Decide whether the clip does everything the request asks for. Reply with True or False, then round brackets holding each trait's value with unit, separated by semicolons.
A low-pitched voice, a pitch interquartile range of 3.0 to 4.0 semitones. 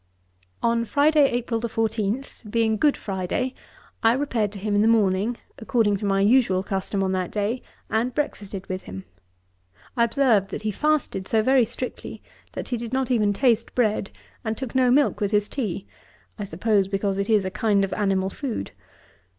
False (220 Hz; 3.7 semitones)